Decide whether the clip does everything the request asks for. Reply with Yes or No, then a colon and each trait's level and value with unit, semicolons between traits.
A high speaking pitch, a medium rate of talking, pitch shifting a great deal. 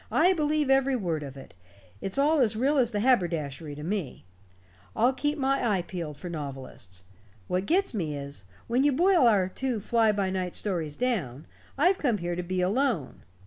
Yes: high, 205 Hz; average, 185 wpm; wide, 8.3 semitones